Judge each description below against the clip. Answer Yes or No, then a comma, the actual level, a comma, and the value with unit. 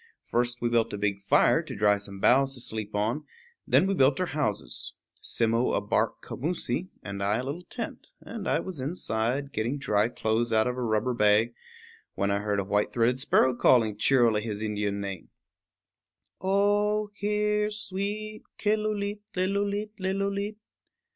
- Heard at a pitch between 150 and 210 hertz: No, low, 125 Hz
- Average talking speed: Yes, average, 160 wpm